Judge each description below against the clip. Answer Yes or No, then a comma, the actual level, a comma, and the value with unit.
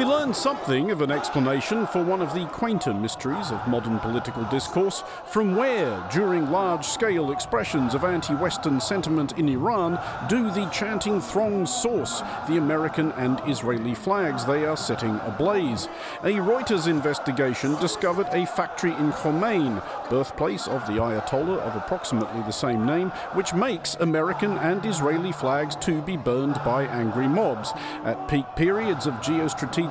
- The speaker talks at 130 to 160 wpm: Yes, average, 155 wpm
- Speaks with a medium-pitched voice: Yes, medium, 155 Hz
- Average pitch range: No, wide, 5.9 semitones